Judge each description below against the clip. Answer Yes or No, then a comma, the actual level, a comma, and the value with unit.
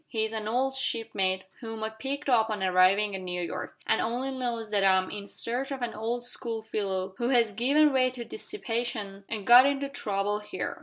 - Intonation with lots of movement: No, average, 3.7 semitones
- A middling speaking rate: No, fast, 210 wpm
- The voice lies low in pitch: No, high, 225 Hz